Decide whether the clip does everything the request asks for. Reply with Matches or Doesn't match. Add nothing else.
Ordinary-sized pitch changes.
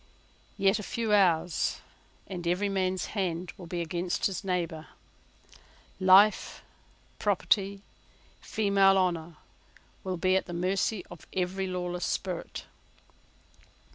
Doesn't match